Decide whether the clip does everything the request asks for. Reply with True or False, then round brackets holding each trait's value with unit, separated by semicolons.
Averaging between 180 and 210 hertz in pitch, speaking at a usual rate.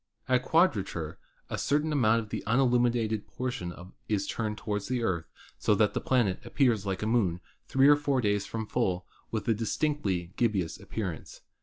False (110 Hz; 170 wpm)